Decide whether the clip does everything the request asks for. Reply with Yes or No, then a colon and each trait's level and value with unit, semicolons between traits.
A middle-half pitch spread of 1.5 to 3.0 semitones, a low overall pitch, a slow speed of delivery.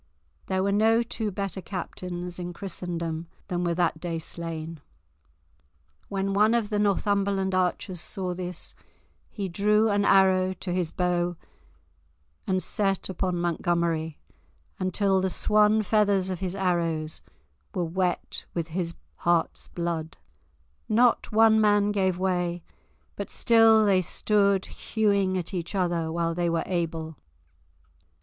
No: average, 2.7 semitones; medium, 185 Hz; slow, 130 wpm